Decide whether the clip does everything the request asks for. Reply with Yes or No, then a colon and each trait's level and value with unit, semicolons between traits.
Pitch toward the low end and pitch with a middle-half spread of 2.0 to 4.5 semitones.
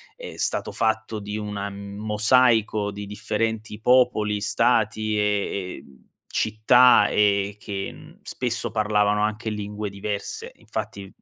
No: low, 105 Hz; narrow, 1.3 semitones